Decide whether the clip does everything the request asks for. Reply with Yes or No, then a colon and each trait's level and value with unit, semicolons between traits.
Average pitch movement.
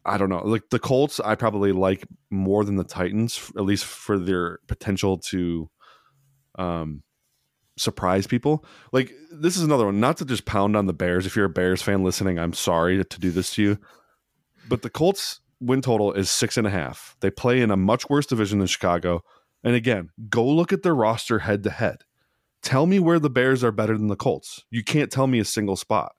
Yes: average, 4.8 semitones